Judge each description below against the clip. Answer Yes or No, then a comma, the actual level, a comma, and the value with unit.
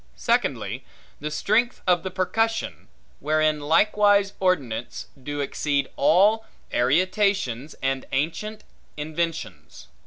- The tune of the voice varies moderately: No, wide, 6.1 semitones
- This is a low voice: No, medium, 160 Hz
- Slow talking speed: Yes, slow, 95 wpm